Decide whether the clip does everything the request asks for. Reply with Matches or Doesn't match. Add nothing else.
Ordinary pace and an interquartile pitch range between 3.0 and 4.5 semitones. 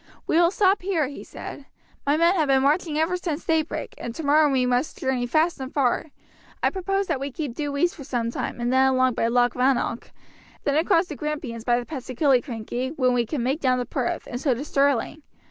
Doesn't match